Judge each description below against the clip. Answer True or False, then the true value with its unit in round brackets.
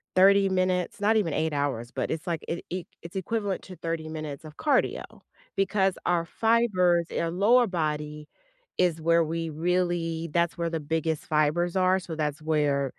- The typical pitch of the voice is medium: True (170 Hz)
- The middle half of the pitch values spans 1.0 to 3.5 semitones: True (2.8 semitones)